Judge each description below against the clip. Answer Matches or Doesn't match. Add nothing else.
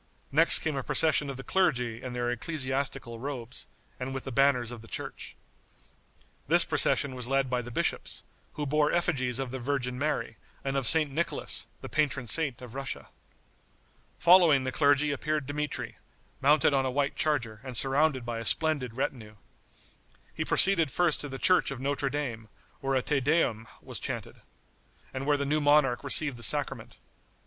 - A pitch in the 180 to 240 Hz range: Doesn't match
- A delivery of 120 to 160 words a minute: Doesn't match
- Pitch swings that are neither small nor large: Matches